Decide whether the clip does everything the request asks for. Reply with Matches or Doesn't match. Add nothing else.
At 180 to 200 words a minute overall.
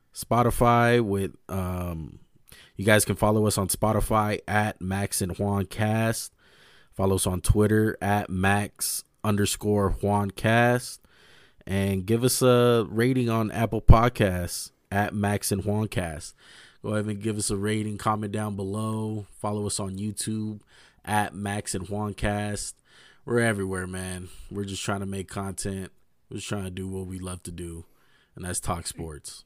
Doesn't match